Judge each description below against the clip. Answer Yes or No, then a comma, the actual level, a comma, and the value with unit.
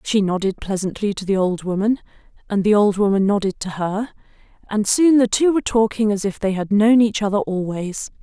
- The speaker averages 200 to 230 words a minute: Yes, fast, 205 wpm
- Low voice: No, high, 210 Hz